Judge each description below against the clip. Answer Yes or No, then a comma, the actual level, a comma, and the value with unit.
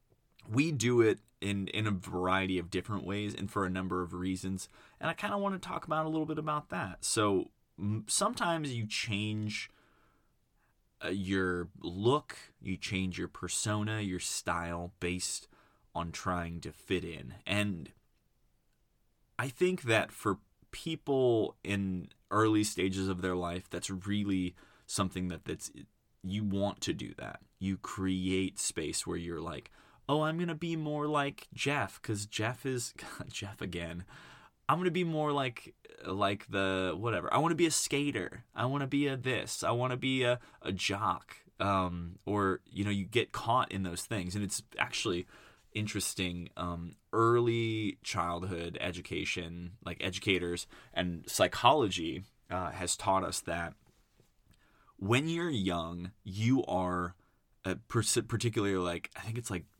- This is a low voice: Yes, low, 100 Hz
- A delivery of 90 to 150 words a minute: No, average, 160 wpm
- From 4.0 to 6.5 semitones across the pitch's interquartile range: Yes, average, 5.0 semitones